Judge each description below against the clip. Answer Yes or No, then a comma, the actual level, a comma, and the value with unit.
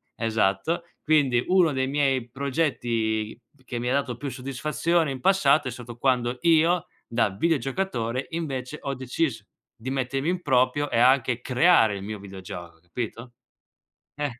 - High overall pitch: No, low, 130 Hz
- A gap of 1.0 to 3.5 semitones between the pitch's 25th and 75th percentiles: No, average, 3.9 semitones